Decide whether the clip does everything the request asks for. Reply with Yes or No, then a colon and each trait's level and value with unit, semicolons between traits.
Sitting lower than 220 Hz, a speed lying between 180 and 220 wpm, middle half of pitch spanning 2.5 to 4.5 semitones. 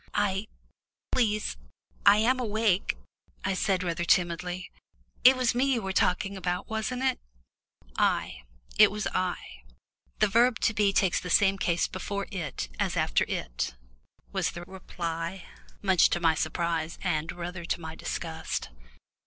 No: medium, 185 Hz; average, 145 wpm; average, 3.6 semitones